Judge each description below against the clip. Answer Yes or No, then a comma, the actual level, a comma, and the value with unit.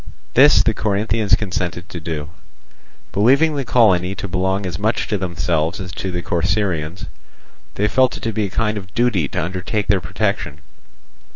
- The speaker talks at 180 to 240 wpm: No, average, 170 wpm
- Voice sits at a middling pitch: No, very low, 95 Hz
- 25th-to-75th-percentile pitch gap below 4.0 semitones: Yes, average, 3.6 semitones